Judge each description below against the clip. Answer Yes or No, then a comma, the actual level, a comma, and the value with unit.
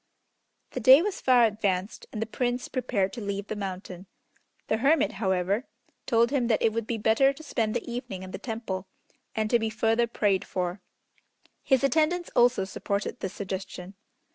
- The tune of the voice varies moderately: Yes, average, 4.1 semitones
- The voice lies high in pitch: Yes, high, 220 Hz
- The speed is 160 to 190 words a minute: Yes, average, 175 wpm